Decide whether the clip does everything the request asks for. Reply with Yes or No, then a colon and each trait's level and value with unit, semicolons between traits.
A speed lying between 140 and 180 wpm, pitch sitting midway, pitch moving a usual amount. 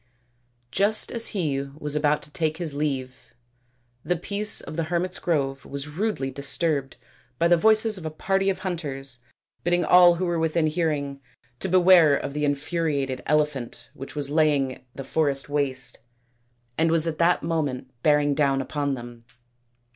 Yes: average, 160 wpm; medium, 150 Hz; average, 3.8 semitones